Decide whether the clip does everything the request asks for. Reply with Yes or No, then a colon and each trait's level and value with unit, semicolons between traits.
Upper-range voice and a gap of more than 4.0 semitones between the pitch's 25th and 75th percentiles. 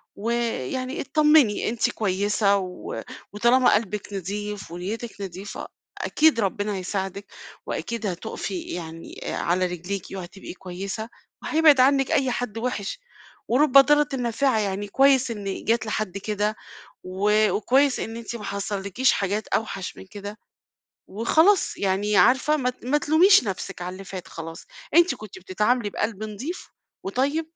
Yes: high, 210 Hz; average, 4.6 semitones